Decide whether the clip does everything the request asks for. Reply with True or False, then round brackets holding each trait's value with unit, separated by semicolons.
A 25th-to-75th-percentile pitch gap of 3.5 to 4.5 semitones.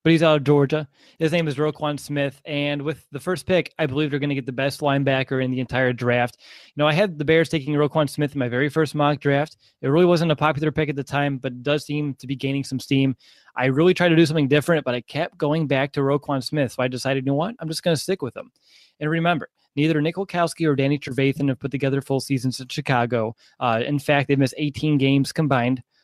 False (2.4 semitones)